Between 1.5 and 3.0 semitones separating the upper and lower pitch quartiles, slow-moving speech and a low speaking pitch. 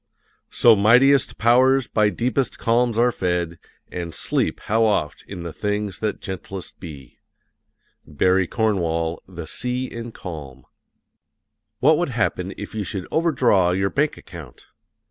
No: wide, 5.4 semitones; slow, 130 wpm; low, 105 Hz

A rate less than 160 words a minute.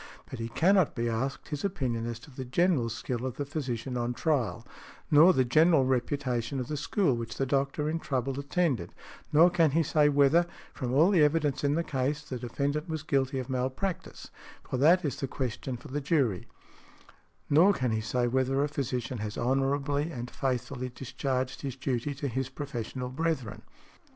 No: average, 185 wpm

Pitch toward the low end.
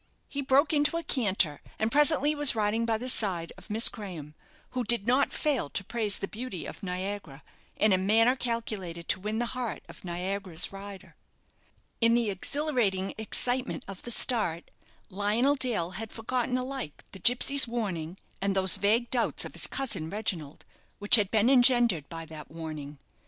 No: high, 215 Hz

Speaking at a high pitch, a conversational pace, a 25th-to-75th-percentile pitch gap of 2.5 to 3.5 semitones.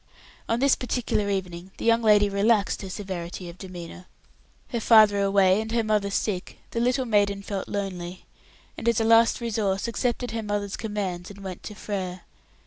Yes: high, 205 Hz; average, 175 wpm; average, 2.9 semitones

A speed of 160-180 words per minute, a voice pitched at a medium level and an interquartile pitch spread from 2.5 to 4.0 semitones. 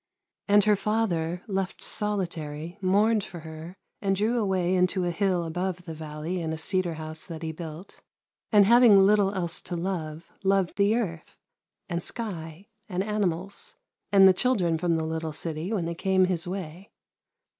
Yes: average, 165 wpm; medium, 180 Hz; average, 3.3 semitones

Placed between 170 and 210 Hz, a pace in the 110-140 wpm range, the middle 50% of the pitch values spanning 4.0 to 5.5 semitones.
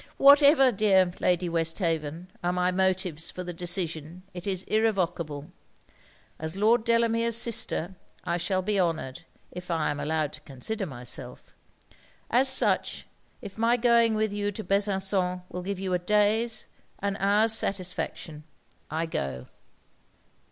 Yes: medium, 185 Hz; slow, 135 wpm; average, 4.3 semitones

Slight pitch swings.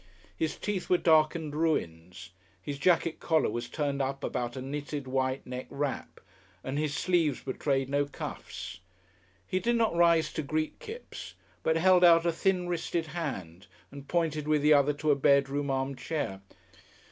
No: average, 3.5 semitones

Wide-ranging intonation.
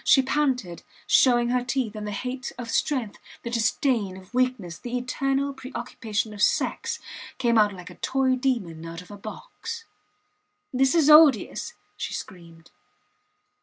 No: average, 4.4 semitones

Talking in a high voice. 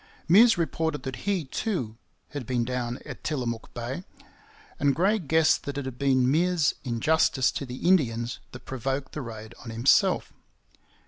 No: low, 135 Hz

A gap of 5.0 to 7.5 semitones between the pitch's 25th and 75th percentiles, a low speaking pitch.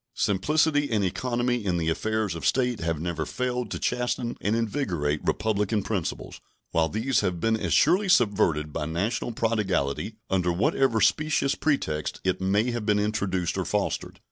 Yes: wide, 5.6 semitones; low, 105 Hz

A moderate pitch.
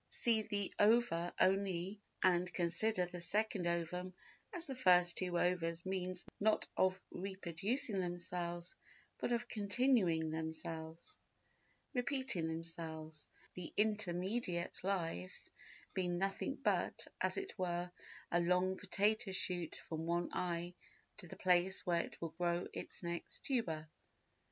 Yes: medium, 180 Hz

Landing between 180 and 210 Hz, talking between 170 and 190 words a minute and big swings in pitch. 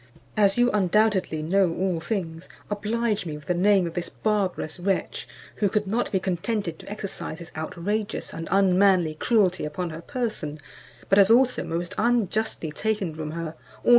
No: high, 190 Hz; average, 175 wpm; average, 4.0 semitones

